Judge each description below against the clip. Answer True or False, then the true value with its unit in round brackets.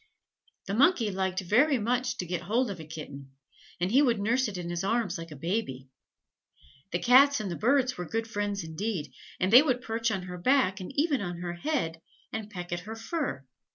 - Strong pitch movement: True (5.8 semitones)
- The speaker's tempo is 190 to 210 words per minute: True (205 wpm)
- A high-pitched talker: True (205 Hz)